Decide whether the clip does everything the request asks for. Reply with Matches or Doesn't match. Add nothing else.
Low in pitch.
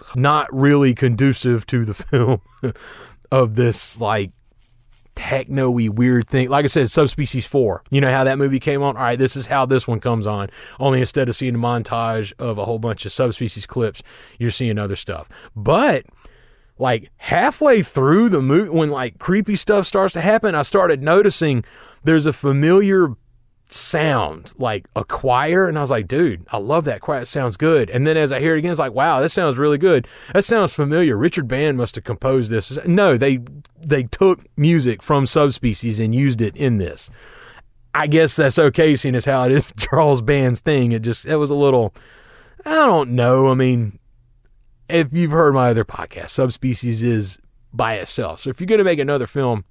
Matches